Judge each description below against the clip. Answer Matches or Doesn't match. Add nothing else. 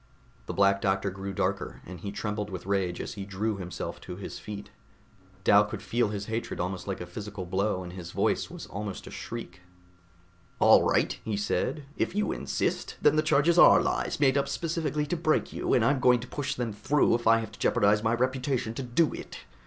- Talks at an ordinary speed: Doesn't match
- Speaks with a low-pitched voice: Matches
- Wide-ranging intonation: Doesn't match